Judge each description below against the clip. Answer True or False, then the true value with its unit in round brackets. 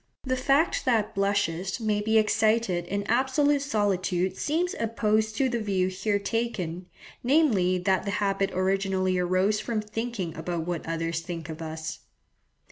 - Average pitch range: True (3.9 semitones)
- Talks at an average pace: True (145 wpm)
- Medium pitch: False (200 Hz)